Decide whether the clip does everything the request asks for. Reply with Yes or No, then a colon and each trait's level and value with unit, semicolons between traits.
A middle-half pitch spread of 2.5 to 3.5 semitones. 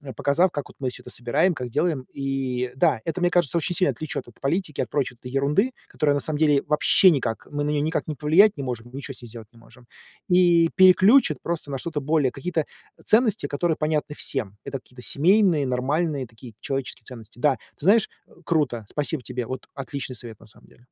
No: average, 4.7 semitones